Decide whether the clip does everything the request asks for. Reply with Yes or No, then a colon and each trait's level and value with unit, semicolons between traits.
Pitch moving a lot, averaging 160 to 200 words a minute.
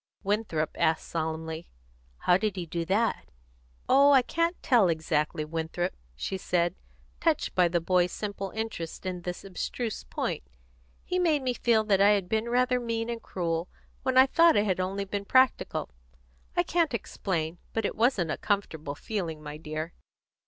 Yes: wide, 5.7 semitones; average, 165 wpm